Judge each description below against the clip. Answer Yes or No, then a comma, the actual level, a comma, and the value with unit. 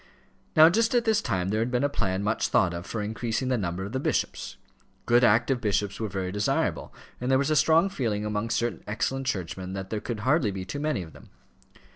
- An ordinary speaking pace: No, fast, 225 wpm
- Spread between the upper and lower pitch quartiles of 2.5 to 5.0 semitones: No, wide, 5.4 semitones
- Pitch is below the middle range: Yes, low, 115 Hz